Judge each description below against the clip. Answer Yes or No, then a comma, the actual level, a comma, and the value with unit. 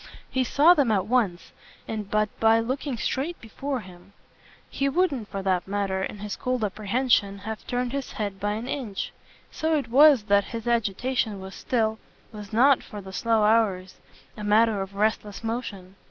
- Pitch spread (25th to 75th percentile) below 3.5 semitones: No, average, 3.9 semitones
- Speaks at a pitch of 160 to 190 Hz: No, high, 220 Hz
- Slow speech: No, average, 175 wpm